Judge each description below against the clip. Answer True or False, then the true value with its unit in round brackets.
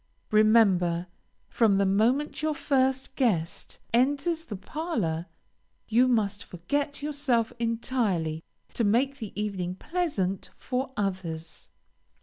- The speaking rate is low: True (110 wpm)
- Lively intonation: True (6.2 semitones)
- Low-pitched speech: False (225 Hz)